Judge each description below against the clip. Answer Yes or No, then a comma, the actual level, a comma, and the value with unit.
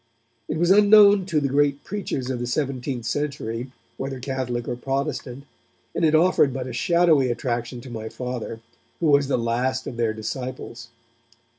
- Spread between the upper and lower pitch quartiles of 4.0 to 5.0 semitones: No, average, 3.3 semitones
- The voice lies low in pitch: Yes, low, 130 Hz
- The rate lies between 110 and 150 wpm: No, average, 165 wpm